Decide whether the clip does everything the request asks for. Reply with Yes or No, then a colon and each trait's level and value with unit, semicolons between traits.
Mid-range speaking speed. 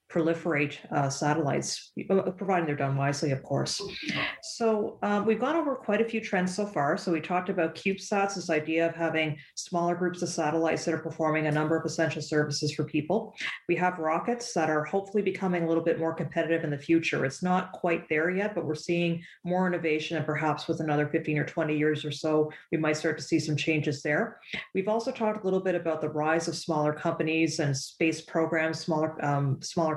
No: fast, 210 wpm